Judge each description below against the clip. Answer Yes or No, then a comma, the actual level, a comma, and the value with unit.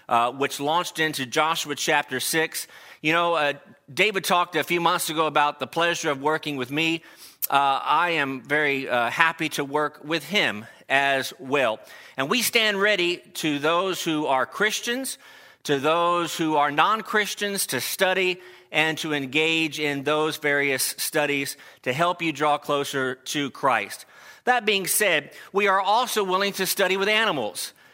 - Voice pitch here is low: No, medium, 160 Hz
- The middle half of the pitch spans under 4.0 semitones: No, average, 4.3 semitones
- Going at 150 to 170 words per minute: Yes, average, 165 wpm